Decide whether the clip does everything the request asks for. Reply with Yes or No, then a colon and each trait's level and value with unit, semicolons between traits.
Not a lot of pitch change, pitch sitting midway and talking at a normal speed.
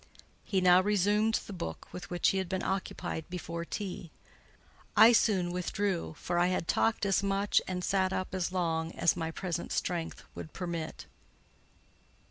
Yes: narrow, 2.3 semitones; medium, 180 Hz; average, 160 wpm